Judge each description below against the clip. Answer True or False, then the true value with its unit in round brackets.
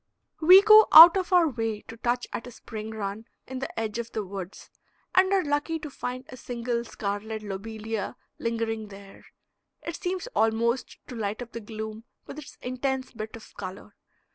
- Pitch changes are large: False (3.7 semitones)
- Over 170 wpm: True (180 wpm)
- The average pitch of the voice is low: False (230 Hz)